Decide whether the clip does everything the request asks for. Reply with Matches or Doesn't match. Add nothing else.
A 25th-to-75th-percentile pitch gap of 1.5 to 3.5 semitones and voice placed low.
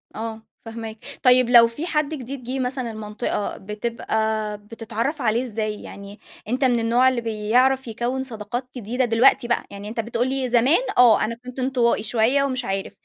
Doesn't match